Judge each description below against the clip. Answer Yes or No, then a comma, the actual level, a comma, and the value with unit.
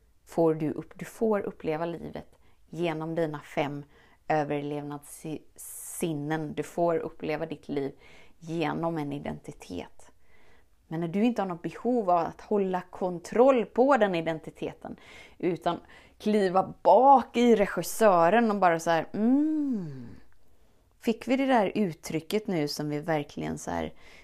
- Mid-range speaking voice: Yes, medium, 165 Hz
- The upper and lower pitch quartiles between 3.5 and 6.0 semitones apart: Yes, wide, 5.6 semitones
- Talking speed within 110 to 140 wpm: Yes, average, 130 wpm